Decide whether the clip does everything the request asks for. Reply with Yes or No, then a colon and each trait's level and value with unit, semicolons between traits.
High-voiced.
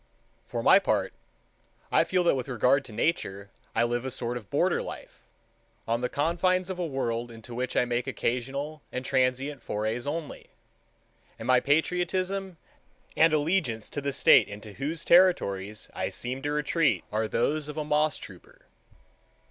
No: low, 135 Hz